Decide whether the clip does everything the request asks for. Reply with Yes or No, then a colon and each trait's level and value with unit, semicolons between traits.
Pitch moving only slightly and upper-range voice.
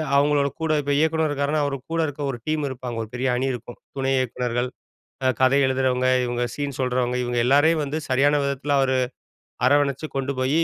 No: narrow, 2.3 semitones; low, 135 Hz